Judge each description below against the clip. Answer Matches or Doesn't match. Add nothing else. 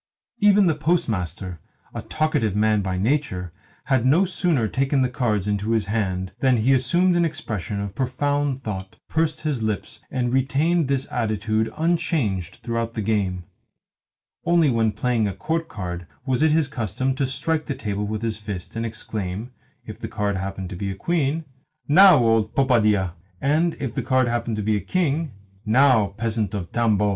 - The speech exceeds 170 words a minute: Matches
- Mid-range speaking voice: Doesn't match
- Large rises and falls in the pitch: Matches